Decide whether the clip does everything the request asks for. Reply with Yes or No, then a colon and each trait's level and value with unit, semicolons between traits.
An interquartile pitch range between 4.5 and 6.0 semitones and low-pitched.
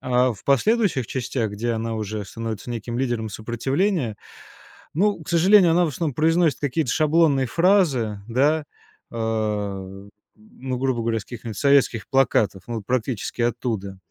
Yes: average, 5.1 semitones; low, 120 Hz